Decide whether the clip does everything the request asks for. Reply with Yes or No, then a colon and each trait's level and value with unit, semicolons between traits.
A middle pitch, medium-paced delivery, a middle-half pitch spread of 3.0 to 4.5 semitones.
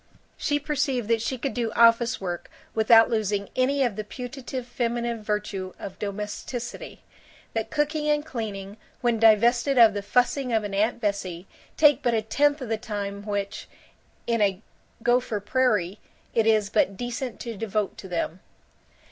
No: high, 225 Hz; average, 160 wpm; average, 3.3 semitones